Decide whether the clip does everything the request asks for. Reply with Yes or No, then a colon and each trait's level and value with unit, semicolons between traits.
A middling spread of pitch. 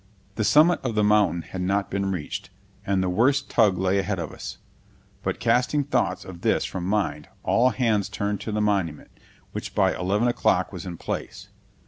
Yes: average, 3.7 semitones